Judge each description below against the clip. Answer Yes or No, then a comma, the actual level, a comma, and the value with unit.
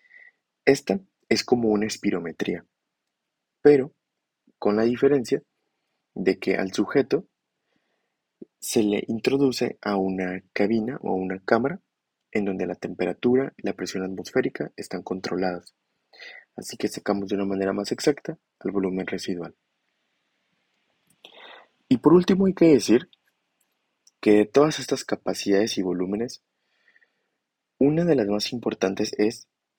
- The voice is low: Yes, low, 105 Hz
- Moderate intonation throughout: No, wide, 6.2 semitones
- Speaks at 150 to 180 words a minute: No, slow, 125 wpm